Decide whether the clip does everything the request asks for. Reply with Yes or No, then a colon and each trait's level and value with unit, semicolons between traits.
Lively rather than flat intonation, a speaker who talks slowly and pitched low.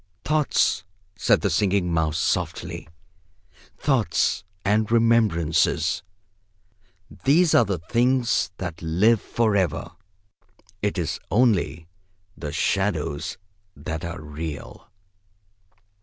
Yes: wide, 6.1 semitones; slow, 95 wpm; very low, 95 Hz